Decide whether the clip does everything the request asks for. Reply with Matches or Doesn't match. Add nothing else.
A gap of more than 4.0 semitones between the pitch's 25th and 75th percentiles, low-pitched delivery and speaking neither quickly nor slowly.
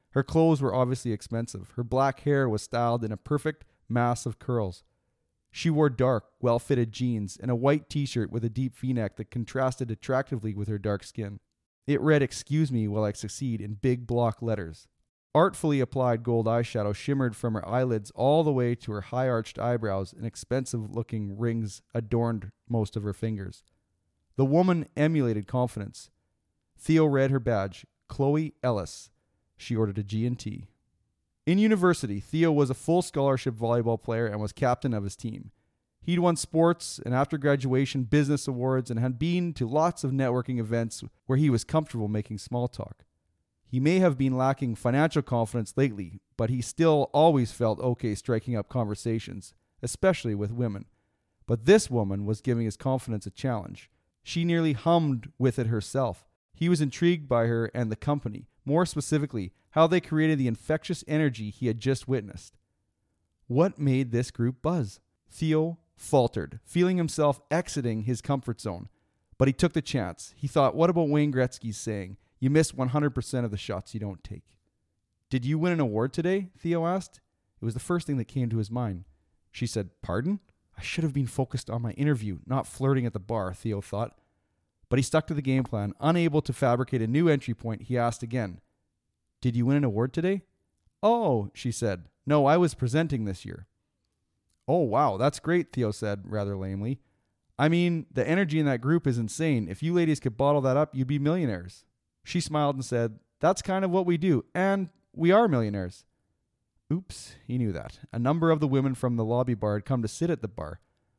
Matches